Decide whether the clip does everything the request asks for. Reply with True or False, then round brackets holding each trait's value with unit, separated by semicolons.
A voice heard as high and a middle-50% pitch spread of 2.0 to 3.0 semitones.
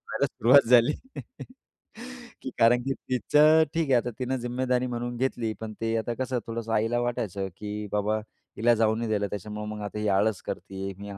False (115 Hz; 2.6 semitones)